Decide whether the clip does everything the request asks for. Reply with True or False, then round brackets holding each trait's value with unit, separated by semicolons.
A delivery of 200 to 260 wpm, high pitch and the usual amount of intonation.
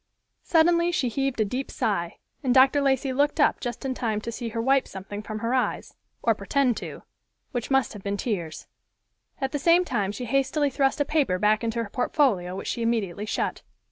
True (205 wpm; 245 Hz; 4.5 semitones)